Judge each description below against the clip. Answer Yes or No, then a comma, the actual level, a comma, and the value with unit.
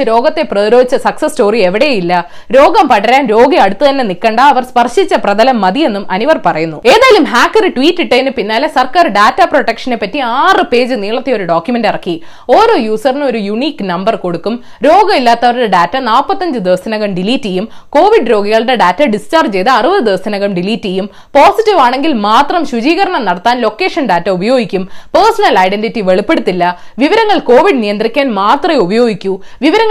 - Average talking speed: Yes, average, 105 wpm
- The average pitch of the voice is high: Yes, high, 240 Hz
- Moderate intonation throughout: No, wide, 6.9 semitones